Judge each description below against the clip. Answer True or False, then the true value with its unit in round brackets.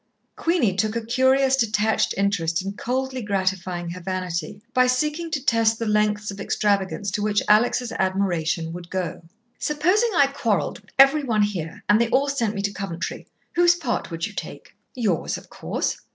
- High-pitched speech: True (210 Hz)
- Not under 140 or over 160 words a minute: False (175 wpm)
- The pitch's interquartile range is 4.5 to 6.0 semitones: True (5.0 semitones)